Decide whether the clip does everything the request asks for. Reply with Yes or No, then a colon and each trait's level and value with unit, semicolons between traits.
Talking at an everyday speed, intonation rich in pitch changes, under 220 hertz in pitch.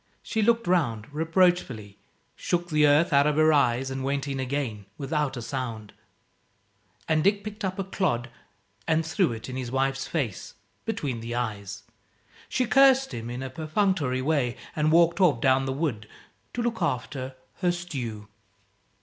Yes: average, 165 wpm; wide, 5.8 semitones; medium, 140 Hz